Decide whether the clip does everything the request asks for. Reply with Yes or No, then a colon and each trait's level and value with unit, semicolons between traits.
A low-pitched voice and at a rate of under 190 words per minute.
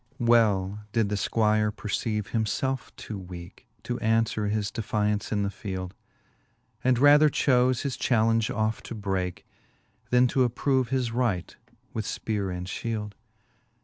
Yes: low, 110 Hz; average, 150 wpm